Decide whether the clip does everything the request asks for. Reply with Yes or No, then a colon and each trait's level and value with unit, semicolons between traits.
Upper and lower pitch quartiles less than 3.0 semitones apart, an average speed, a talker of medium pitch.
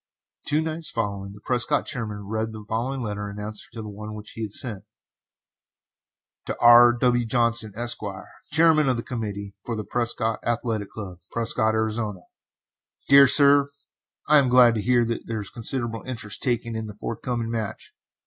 No: narrow, 2.5 semitones; average, 170 wpm; low, 115 Hz